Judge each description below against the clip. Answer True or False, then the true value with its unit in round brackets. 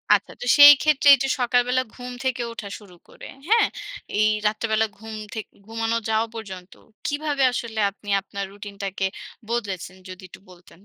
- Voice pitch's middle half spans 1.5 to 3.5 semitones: False (3.9 semitones)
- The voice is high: True (220 Hz)